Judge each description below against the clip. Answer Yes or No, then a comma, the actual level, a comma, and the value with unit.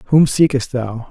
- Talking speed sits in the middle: Yes, average, 165 wpm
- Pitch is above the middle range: No, low, 130 Hz